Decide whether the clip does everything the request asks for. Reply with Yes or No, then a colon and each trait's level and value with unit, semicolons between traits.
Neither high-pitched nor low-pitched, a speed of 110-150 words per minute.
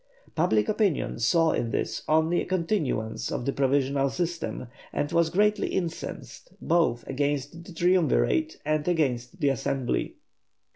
Yes: medium, 160 Hz; slow, 135 wpm